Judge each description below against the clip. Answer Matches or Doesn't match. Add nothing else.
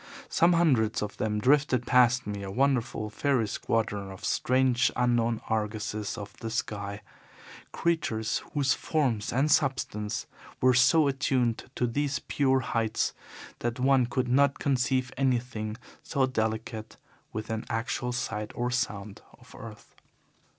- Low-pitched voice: Matches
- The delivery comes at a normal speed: Doesn't match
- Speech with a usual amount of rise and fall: Matches